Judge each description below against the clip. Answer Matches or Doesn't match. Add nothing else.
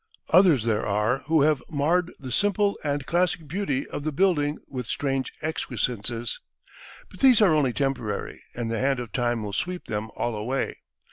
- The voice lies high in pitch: Doesn't match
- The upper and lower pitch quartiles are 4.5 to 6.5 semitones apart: Matches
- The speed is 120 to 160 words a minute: Doesn't match